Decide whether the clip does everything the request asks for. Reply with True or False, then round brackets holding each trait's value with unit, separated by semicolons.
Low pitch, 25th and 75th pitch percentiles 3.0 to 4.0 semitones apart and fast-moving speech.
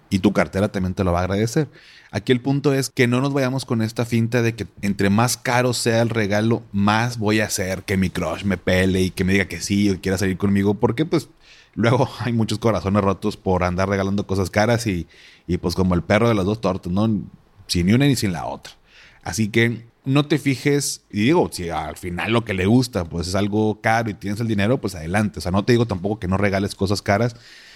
True (105 Hz; 3.5 semitones; 240 wpm)